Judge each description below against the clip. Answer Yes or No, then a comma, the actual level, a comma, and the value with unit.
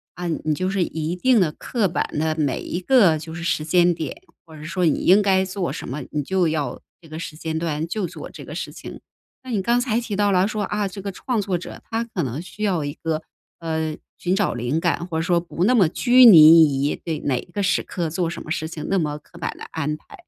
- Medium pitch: Yes, medium, 170 Hz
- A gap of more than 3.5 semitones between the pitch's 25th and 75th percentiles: Yes, average, 3.9 semitones